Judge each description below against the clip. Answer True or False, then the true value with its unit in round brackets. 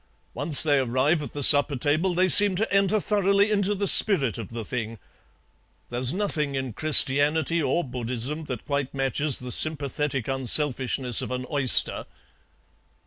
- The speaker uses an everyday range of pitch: True (4.9 semitones)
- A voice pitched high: False (145 Hz)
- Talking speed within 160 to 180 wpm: False (150 wpm)